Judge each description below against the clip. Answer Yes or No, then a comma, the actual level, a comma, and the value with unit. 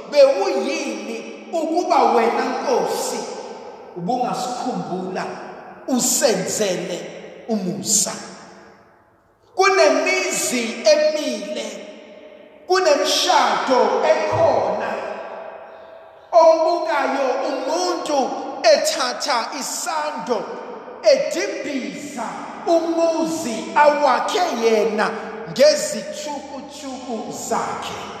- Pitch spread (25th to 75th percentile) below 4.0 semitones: No, average, 4.7 semitones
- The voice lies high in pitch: Yes, very high, 290 Hz